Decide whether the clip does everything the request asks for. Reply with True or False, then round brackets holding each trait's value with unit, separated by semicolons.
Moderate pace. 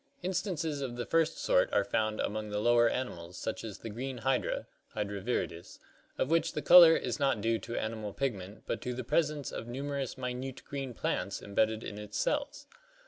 True (195 wpm)